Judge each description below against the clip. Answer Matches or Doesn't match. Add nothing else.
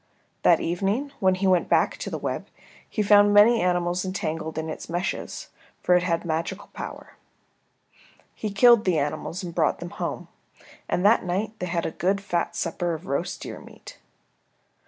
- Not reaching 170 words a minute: Doesn't match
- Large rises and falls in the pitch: Doesn't match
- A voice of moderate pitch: Matches